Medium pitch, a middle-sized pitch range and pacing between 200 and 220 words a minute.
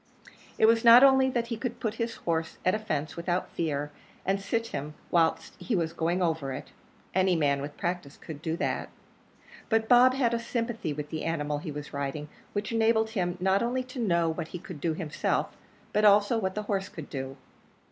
No: medium, 180 Hz; wide, 6.3 semitones; fast, 205 wpm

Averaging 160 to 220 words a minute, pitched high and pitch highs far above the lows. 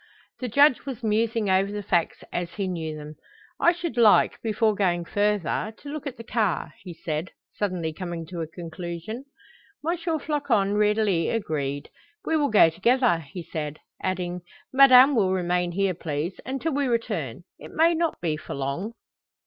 Yes: average, 165 wpm; high, 195 Hz; wide, 6.0 semitones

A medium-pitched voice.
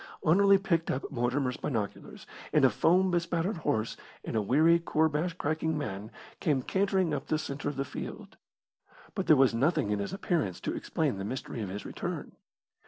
Yes: medium, 150 Hz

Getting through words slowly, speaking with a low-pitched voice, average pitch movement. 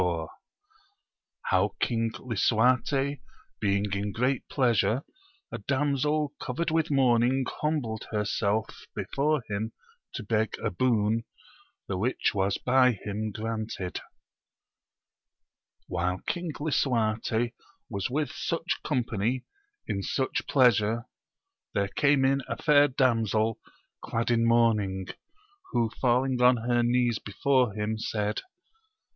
Yes: slow, 110 wpm; low, 120 Hz; average, 3.7 semitones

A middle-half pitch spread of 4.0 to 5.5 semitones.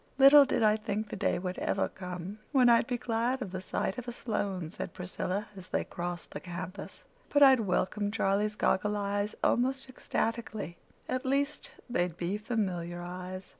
Yes: average, 4.6 semitones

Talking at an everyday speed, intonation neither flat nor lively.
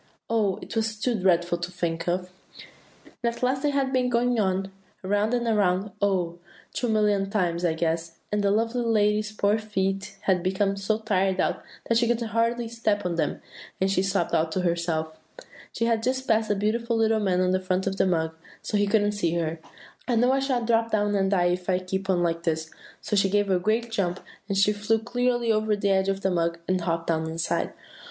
No: fast, 220 wpm; average, 3.6 semitones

